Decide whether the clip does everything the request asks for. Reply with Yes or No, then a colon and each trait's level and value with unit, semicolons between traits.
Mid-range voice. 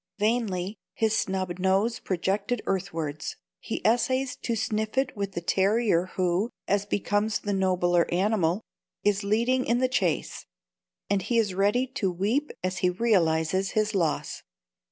No: high, 200 Hz